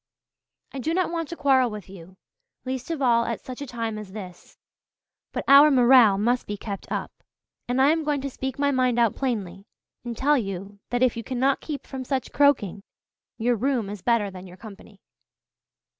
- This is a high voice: Yes, high, 245 Hz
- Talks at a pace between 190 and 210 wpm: Yes, average, 195 wpm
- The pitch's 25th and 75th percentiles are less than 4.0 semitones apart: No, average, 4.7 semitones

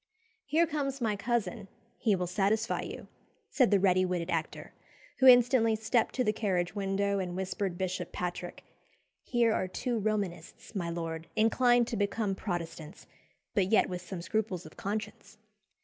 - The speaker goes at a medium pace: Yes, average, 155 wpm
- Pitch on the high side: Yes, high, 200 Hz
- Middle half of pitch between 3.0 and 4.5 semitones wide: Yes, average, 3.9 semitones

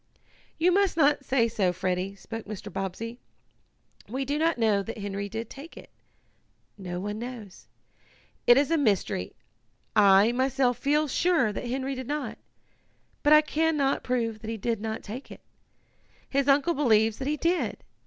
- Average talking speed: Yes, average, 165 wpm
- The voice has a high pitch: Yes, high, 240 Hz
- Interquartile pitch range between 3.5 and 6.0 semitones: Yes, average, 5.3 semitones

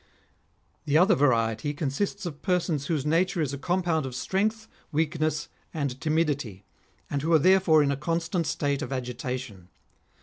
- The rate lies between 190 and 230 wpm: No, average, 155 wpm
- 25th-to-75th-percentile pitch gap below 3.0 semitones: No, average, 3.9 semitones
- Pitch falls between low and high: Yes, medium, 150 Hz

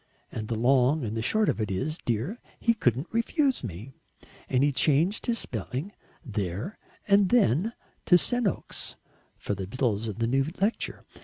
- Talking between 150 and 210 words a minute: Yes, average, 165 wpm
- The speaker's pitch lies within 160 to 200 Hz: No, low, 135 Hz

